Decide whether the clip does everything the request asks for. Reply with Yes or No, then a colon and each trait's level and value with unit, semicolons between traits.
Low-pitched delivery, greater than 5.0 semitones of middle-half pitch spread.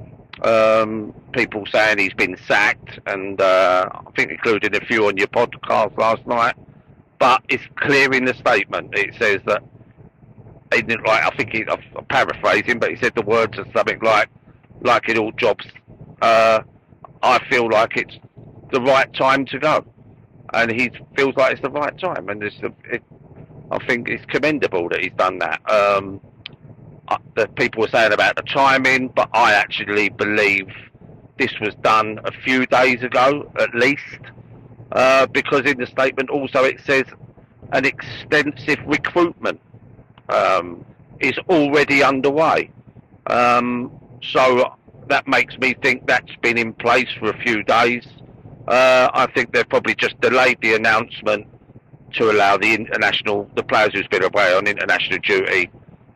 No: low, 125 Hz; average, 3.5 semitones